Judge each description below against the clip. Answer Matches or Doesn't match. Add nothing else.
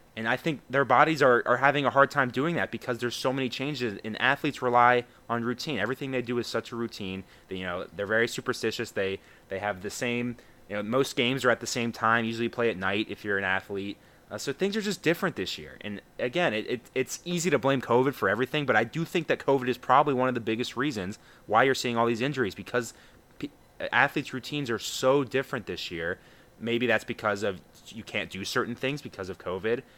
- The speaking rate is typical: Doesn't match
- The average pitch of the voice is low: Matches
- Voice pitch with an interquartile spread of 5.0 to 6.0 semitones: Doesn't match